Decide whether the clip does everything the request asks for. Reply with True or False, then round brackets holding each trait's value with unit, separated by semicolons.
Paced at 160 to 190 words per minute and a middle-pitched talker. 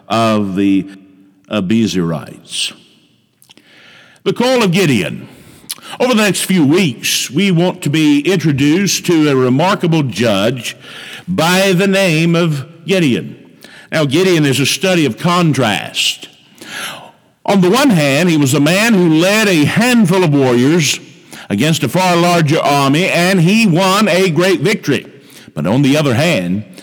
False (140 wpm; 165 Hz)